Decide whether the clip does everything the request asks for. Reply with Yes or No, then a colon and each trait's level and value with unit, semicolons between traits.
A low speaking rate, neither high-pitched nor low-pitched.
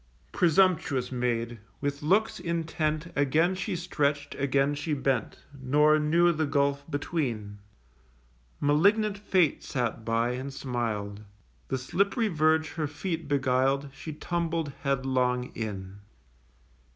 Yes: slow, 115 wpm; medium, 145 Hz